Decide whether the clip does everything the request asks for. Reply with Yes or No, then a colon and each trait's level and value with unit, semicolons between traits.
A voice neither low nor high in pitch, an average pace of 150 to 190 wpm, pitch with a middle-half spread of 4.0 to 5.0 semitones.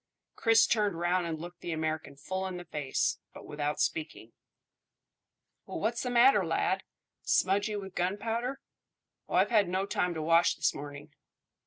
Yes: medium, 180 Hz; average, 160 wpm; average, 4.7 semitones